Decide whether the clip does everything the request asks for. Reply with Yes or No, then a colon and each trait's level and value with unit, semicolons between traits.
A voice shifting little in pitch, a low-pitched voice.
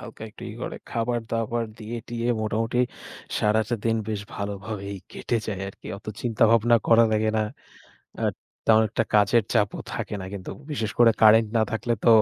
Yes: narrow, 1.7 semitones; low, 110 Hz